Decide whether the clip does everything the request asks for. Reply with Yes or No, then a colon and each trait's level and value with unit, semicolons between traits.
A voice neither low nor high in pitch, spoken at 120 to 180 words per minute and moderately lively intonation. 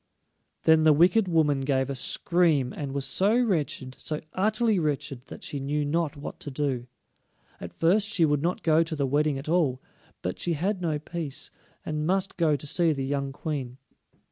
No: medium, 150 Hz; average, 190 wpm; average, 3.7 semitones